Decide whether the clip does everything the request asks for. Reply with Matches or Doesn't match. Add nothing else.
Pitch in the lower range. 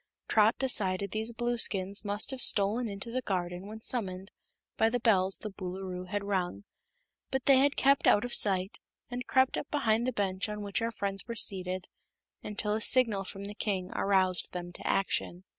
Doesn't match